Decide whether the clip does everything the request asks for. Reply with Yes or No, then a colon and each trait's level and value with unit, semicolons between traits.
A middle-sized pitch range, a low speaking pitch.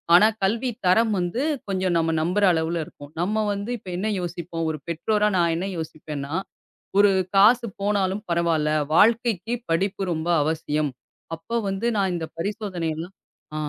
No: average, 4.1 semitones; medium, 185 Hz